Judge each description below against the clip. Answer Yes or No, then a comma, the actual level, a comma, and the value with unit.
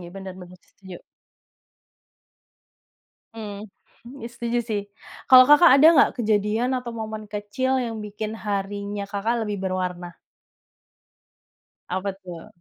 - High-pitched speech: Yes, high, 210 Hz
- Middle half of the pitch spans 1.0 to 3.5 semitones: Yes, average, 2.9 semitones